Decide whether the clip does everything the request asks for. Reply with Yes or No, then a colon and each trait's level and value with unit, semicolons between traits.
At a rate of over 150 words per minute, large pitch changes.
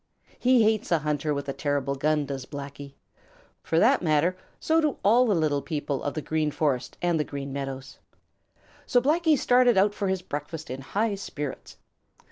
Yes: average, 180 wpm; wide, 6.6 semitones